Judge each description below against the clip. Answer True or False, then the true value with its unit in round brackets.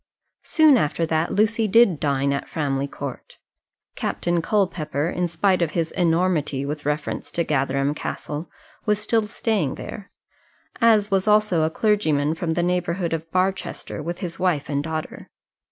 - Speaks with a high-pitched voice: False (170 Hz)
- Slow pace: False (155 wpm)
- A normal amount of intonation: True (4.5 semitones)